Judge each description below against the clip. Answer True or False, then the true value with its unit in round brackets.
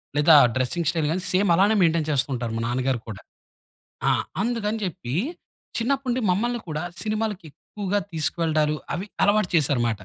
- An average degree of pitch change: False (6.2 semitones)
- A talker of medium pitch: True (170 Hz)